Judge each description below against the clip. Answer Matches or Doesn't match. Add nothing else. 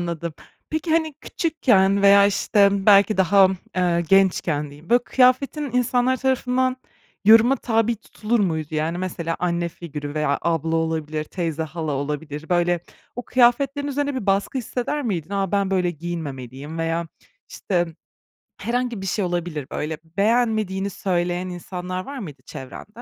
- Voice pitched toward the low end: Doesn't match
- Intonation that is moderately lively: Doesn't match